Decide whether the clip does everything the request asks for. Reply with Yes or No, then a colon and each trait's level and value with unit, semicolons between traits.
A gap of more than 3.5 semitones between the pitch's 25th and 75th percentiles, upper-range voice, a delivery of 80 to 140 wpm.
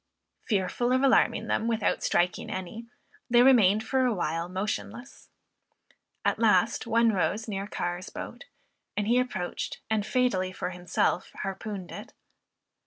Yes: average, 4.1 semitones; high, 210 Hz; slow, 135 wpm